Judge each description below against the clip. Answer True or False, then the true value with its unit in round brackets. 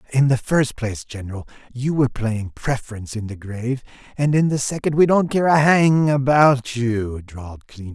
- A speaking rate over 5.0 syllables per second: True (5.4 syllables/s)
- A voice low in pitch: True (125 Hz)